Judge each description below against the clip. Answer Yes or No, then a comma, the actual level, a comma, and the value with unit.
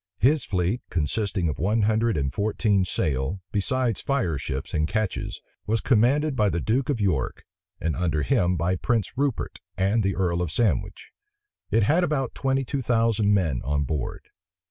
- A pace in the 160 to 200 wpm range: Yes, average, 165 wpm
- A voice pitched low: Yes, low, 105 Hz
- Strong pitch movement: Yes, wide, 5.7 semitones